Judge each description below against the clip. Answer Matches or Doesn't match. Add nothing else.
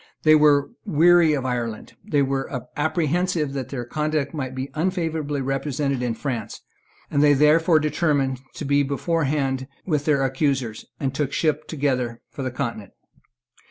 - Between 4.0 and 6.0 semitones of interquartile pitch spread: Doesn't match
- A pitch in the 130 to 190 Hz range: Matches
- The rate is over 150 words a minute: Doesn't match